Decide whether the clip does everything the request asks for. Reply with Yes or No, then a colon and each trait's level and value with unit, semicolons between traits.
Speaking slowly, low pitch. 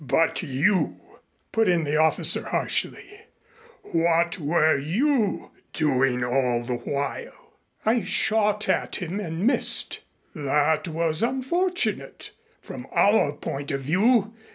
No: slow, 115 wpm; medium, 165 Hz